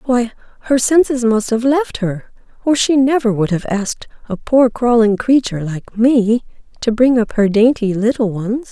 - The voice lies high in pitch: Yes, high, 235 Hz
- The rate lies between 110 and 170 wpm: No, average, 180 wpm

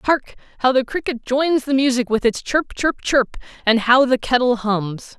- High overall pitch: Yes, very high, 250 Hz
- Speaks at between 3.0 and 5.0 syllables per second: Yes, 4.7 syllables/s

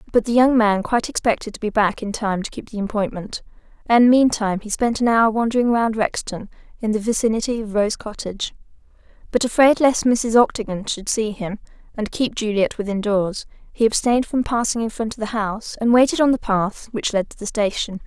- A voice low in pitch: No, high, 220 Hz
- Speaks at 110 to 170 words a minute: No, fast, 205 wpm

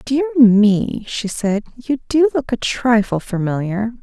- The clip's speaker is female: Yes, female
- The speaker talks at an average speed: Yes, average, 150 wpm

